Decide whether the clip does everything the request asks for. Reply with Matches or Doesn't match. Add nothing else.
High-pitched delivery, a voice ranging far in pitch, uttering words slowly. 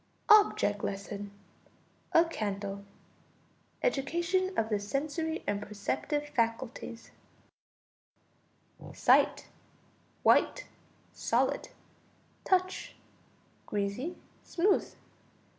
Matches